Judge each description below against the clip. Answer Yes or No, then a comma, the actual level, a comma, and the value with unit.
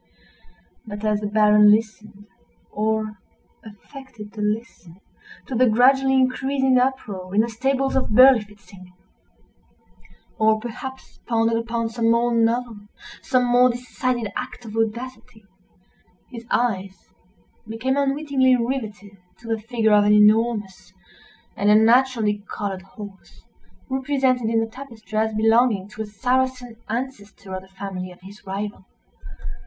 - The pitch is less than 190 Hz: No, high, 225 Hz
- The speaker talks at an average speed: No, slow, 125 wpm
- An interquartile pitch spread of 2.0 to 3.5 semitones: Yes, average, 3.2 semitones